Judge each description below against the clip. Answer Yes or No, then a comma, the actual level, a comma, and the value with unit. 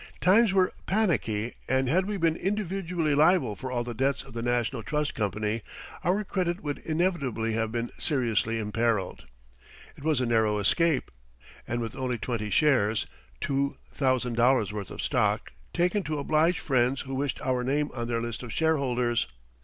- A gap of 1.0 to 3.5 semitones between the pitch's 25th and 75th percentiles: No, wide, 5.6 semitones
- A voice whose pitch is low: Yes, low, 130 Hz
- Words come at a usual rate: Yes, average, 170 wpm